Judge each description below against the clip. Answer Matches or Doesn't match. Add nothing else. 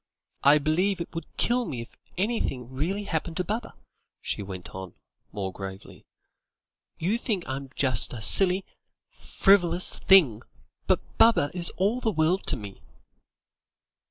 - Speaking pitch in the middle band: Matches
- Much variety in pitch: Matches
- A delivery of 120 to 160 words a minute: Matches